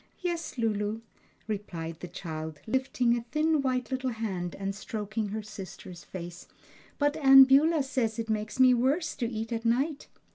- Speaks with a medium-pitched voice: No, high, 225 Hz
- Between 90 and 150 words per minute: No, average, 160 wpm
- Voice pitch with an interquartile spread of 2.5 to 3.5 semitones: No, average, 4.6 semitones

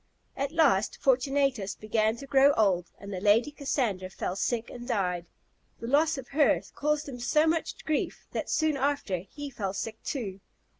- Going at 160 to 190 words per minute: Yes, average, 170 wpm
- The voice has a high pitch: Yes, high, 245 Hz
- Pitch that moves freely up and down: Yes, wide, 6.0 semitones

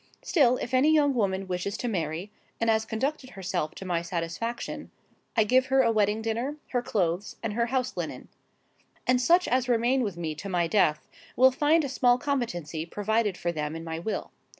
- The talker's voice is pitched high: Yes, high, 220 Hz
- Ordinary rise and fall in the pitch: No, wide, 6.3 semitones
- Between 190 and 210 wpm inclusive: Yes, average, 195 wpm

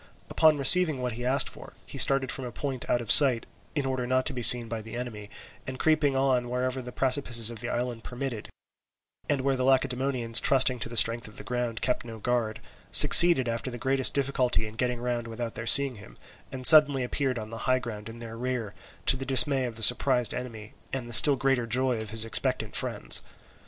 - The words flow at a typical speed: No, fast, 215 wpm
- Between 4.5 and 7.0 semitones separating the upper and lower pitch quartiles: No, narrow, 2.4 semitones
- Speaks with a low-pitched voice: Yes, low, 125 Hz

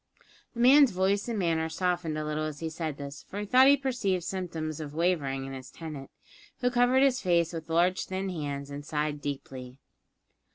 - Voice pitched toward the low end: No, medium, 165 Hz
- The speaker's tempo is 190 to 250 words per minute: Yes, average, 200 wpm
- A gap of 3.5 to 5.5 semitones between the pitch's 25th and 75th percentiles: Yes, average, 4.7 semitones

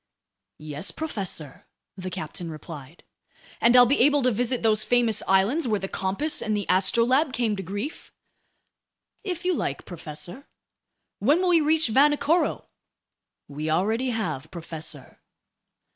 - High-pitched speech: Yes, high, 215 Hz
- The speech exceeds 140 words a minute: No, slow, 135 wpm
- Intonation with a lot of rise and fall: Yes, wide, 7.8 semitones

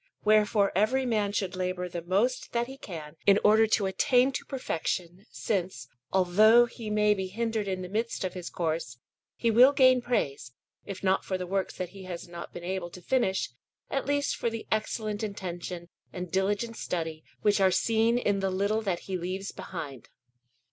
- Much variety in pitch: No, average, 3.6 semitones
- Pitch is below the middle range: No, high, 195 Hz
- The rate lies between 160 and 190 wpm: Yes, average, 185 wpm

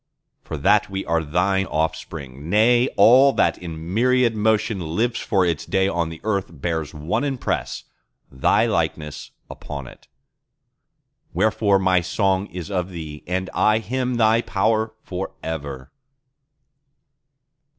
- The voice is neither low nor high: No, very low, 95 Hz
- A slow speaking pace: Yes, slow, 125 wpm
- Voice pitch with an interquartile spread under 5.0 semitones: No, average, 5.3 semitones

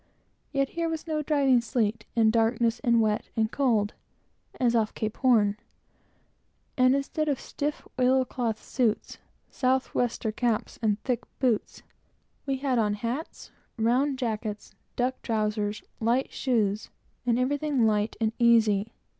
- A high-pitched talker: Yes, high, 235 Hz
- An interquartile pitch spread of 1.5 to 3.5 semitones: Yes, average, 3.2 semitones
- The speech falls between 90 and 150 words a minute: Yes, average, 140 wpm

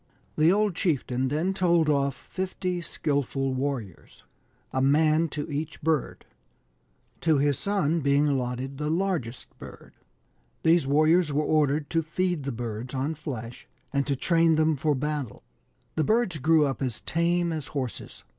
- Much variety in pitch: No, average, 3.3 semitones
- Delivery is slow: No, average, 150 wpm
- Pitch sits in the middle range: Yes, medium, 150 Hz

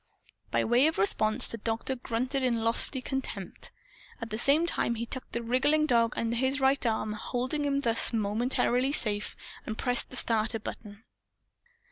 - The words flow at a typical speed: Yes, average, 170 wpm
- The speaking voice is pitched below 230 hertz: No, high, 240 Hz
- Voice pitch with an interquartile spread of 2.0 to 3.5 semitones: Yes, average, 2.8 semitones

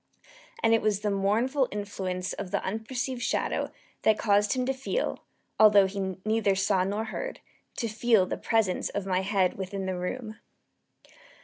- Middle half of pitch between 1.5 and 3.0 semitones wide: Yes, average, 2.7 semitones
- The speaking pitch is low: No, high, 205 Hz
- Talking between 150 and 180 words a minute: Yes, average, 165 wpm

